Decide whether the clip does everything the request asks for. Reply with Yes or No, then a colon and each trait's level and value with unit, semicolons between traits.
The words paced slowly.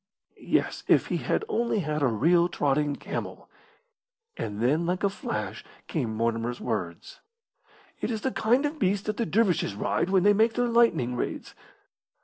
No: average, 165 wpm